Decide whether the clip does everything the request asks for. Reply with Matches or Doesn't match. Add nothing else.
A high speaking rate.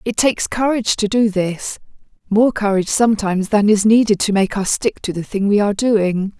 Doesn't match